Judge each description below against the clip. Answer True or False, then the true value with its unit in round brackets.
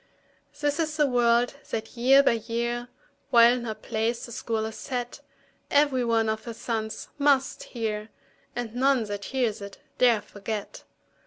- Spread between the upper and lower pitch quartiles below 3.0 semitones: True (2.5 semitones)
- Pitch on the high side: True (235 Hz)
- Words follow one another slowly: False (160 wpm)